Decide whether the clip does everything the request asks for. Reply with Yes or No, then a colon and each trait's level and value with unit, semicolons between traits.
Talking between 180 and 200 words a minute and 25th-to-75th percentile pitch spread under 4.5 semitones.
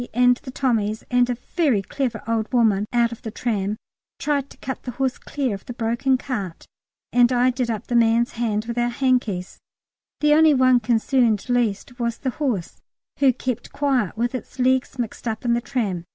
Yes: average, 195 wpm; narrow, 2.5 semitones